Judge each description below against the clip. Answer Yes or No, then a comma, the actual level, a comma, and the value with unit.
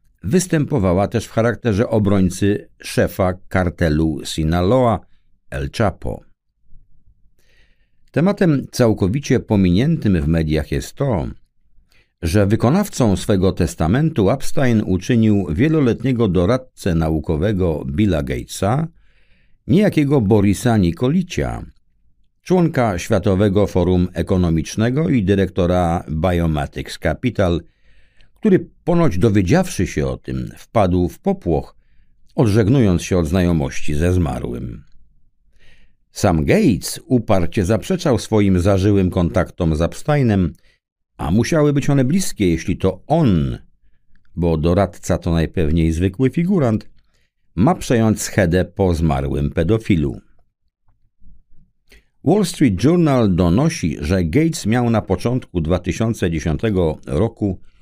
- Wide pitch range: Yes, wide, 6.0 semitones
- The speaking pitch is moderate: No, low, 100 Hz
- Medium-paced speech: No, slow, 100 wpm